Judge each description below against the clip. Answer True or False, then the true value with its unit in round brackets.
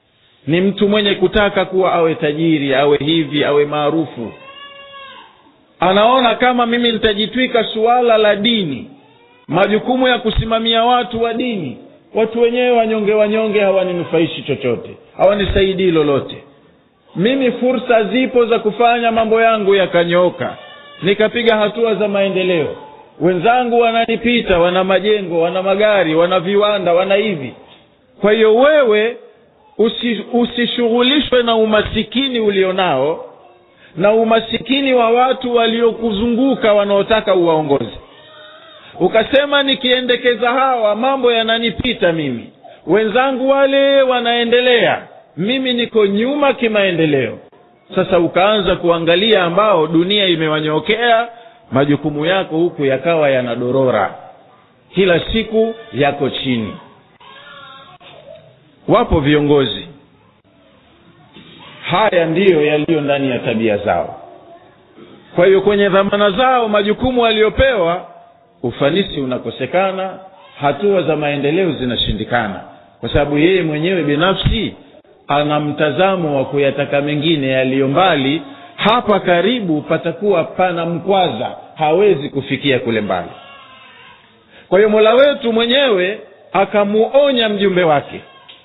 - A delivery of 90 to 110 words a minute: True (100 wpm)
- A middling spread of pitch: False (6.3 semitones)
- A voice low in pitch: False (205 Hz)